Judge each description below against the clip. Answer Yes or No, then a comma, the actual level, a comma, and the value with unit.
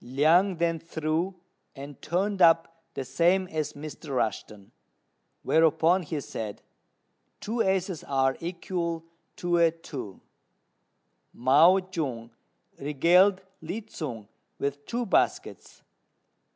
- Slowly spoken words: Yes, slow, 105 wpm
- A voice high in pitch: No, medium, 165 Hz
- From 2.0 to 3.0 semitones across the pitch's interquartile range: No, average, 4.1 semitones